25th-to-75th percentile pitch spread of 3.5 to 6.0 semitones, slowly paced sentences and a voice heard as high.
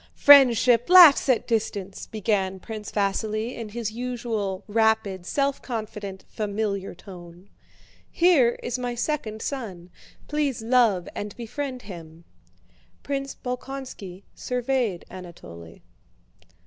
Yes: average, 4.4 semitones; slow, 105 wpm; high, 220 Hz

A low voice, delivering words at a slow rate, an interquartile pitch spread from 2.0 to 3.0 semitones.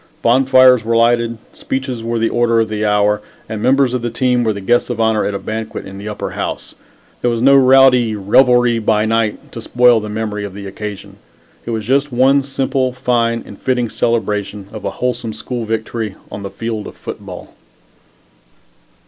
No: low, 115 Hz; average, 190 wpm; average, 2.7 semitones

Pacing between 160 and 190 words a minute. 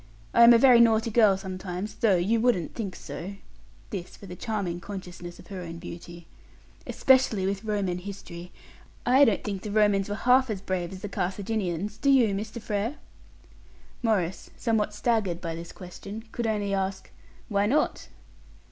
Yes: average, 165 wpm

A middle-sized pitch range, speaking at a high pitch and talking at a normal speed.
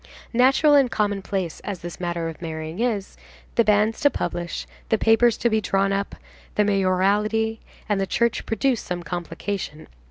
Yes: average, 4.0 semitones; high, 200 Hz; average, 160 wpm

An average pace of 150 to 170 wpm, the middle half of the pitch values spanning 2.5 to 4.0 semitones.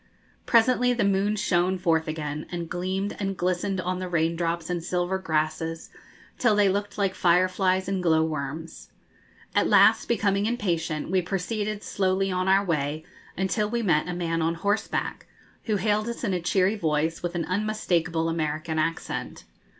Yes: average, 160 wpm; average, 3.4 semitones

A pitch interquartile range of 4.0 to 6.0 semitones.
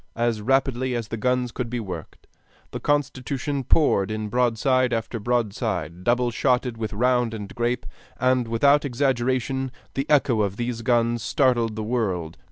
No: narrow, 2.4 semitones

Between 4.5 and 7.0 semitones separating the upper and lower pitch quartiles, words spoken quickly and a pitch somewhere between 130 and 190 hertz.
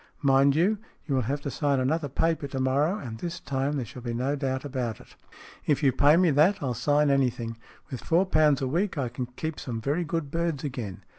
No: average, 3.3 semitones; fast, 230 wpm; medium, 140 Hz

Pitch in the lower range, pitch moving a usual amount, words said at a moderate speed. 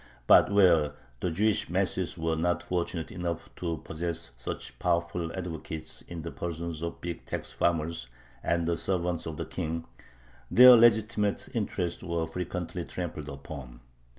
No: very low, 85 Hz; narrow, 1.8 semitones; average, 145 wpm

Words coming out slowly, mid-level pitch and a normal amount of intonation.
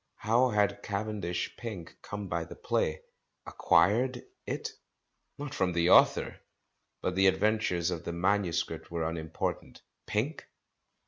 No: slow, 125 wpm; very low, 95 Hz; average, 4.0 semitones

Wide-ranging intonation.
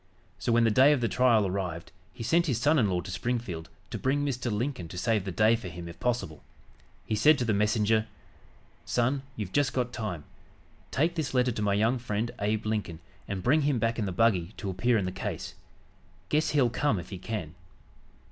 No: average, 4.4 semitones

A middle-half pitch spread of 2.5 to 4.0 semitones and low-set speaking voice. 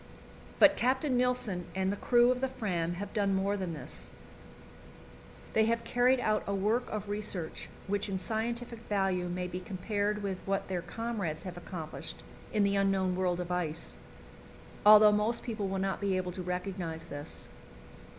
No: average, 3.3 semitones; high, 195 Hz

